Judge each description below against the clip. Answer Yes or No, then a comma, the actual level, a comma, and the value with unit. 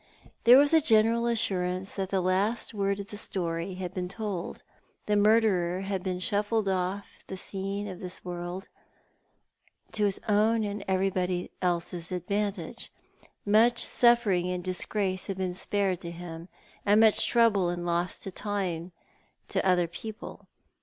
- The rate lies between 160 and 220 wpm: No, average, 150 wpm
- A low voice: No, high, 195 Hz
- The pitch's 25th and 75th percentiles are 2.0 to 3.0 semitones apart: Yes, narrow, 2.6 semitones